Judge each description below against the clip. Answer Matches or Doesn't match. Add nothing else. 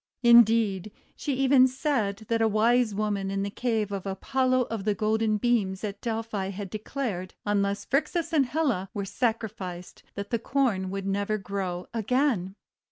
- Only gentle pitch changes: Doesn't match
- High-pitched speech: Matches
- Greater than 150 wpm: Matches